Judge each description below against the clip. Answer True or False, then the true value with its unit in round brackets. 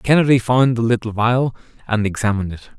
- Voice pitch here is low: True (115 Hz)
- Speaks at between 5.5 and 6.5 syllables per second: True (5.9 syllables/s)